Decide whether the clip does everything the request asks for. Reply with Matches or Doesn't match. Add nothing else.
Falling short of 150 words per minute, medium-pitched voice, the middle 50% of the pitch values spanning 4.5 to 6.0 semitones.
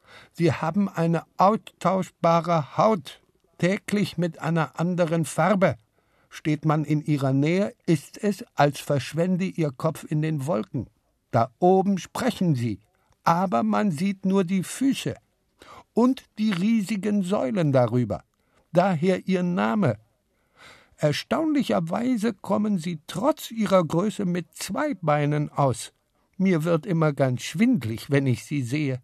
Matches